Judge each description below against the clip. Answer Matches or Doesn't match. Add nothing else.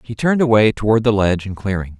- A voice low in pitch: Matches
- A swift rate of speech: Matches